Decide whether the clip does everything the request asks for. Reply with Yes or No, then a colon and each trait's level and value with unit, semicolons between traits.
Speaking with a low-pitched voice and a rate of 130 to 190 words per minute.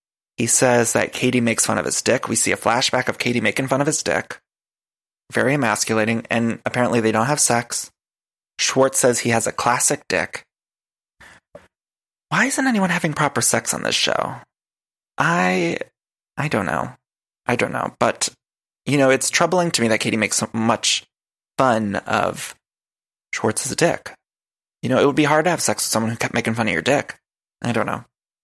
Yes: low, 120 Hz; average, 185 wpm